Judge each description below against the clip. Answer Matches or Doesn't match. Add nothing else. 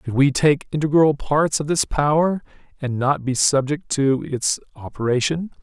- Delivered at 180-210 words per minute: Doesn't match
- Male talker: Matches